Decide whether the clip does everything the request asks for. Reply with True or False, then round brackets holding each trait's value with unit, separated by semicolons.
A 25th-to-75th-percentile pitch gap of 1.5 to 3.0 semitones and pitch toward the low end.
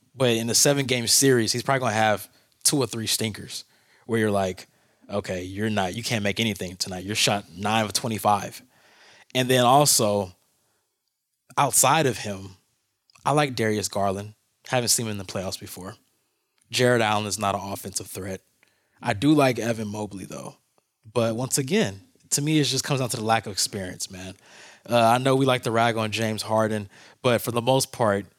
False (3.6 semitones; 110 Hz)